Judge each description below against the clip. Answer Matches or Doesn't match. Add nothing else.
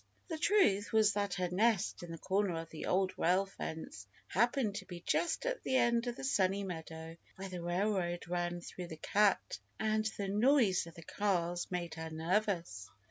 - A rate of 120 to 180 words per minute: Doesn't match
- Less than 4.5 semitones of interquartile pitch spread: Matches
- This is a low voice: Doesn't match